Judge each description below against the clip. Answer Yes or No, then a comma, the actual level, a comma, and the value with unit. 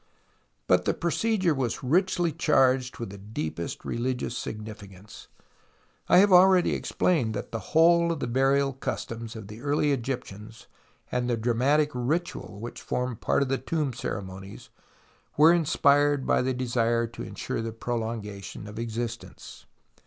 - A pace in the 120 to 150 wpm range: Yes, average, 145 wpm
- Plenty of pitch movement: No, average, 4.6 semitones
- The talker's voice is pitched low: Yes, low, 125 Hz